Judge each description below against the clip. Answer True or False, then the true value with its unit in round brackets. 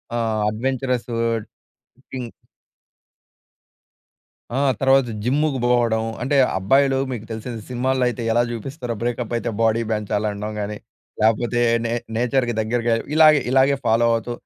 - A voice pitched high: False (120 Hz)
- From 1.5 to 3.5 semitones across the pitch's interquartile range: True (2.8 semitones)